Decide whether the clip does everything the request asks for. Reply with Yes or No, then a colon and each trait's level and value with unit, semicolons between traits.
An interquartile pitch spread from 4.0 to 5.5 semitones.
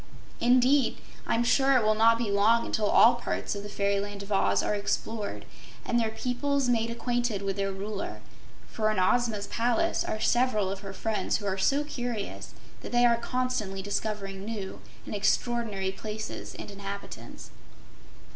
No: average, 3.1 semitones